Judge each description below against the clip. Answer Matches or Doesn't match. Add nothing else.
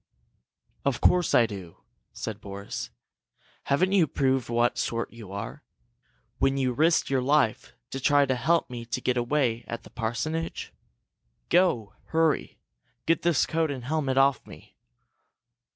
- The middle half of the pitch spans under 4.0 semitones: Doesn't match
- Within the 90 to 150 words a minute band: Matches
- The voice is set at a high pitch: Doesn't match